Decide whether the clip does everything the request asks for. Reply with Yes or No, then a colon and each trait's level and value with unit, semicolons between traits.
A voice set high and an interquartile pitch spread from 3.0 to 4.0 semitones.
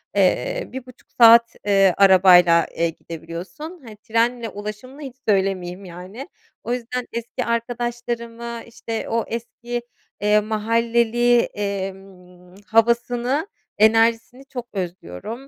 Yes: high, 230 Hz; average, 3.6 semitones